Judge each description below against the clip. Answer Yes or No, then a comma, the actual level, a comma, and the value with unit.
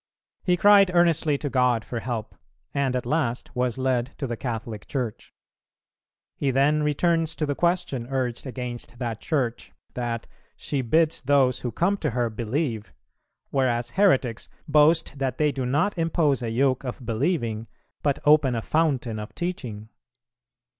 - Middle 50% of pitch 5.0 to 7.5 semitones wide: No, average, 4.2 semitones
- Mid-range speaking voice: No, low, 130 Hz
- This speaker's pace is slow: No, average, 155 wpm